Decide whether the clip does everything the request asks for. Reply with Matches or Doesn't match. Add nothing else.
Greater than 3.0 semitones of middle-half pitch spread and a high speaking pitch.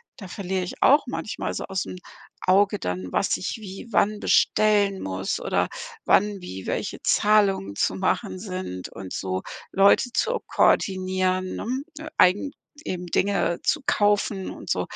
Doesn't match